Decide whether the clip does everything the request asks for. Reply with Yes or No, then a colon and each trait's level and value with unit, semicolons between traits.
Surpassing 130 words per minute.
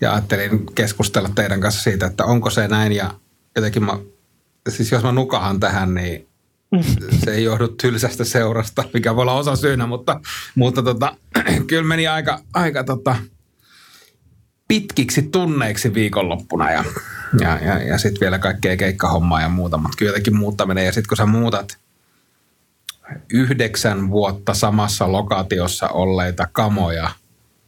Yes: average, 140 wpm